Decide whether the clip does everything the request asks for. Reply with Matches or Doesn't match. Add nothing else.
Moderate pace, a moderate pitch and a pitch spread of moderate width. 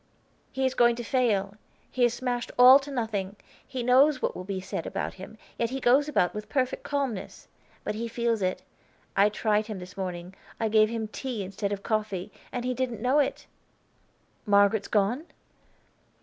Doesn't match